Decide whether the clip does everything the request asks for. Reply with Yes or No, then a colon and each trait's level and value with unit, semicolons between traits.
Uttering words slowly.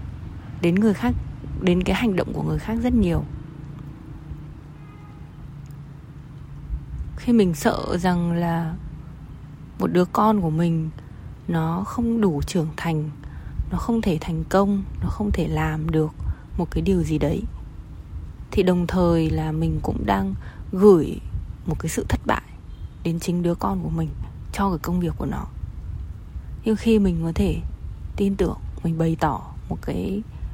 Yes: slow, 155 wpm